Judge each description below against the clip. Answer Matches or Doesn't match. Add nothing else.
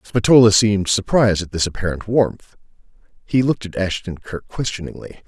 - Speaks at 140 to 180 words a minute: Matches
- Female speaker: Doesn't match